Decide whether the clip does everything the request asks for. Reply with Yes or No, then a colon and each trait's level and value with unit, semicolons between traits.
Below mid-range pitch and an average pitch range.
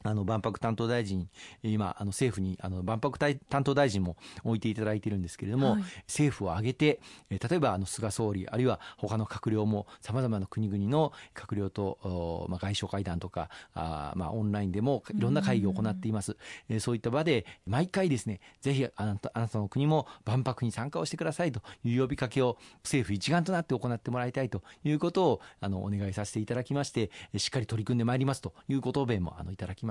Yes: low, 110 Hz; average, 4.8 semitones